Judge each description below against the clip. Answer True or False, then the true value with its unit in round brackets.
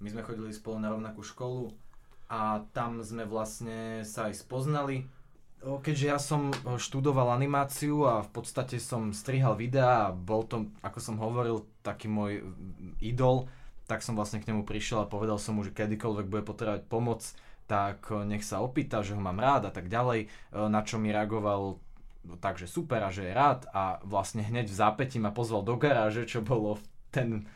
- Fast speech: True (180 wpm)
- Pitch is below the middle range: True (110 Hz)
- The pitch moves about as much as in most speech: True (3.0 semitones)